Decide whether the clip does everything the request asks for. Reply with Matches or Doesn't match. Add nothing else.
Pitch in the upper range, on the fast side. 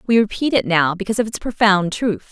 Matches